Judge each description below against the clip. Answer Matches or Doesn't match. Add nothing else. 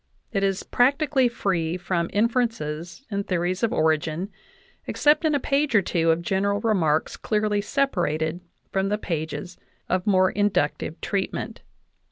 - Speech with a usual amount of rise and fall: Matches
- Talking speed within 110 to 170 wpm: Matches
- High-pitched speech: Matches